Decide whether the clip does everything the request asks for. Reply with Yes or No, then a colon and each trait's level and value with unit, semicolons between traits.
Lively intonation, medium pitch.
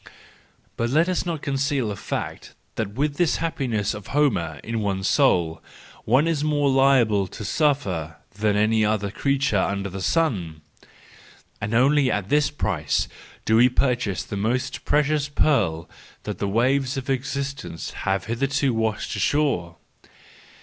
No: wide, 5.8 semitones; low, 120 Hz